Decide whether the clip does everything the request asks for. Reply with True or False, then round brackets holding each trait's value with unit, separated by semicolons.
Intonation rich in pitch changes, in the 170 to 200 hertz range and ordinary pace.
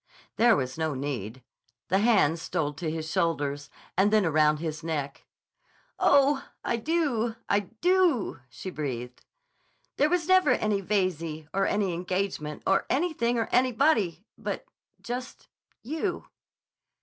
False (7.8 semitones; 190 Hz; 120 wpm)